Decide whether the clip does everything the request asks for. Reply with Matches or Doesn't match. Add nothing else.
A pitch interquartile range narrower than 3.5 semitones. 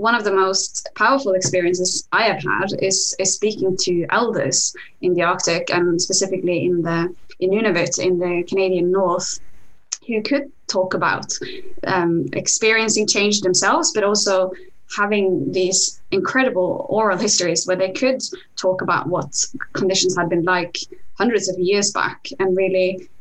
Matches